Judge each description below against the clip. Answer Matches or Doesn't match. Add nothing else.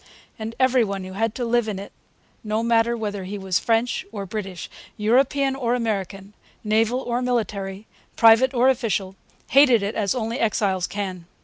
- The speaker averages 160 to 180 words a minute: Matches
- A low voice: Doesn't match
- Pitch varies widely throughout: Doesn't match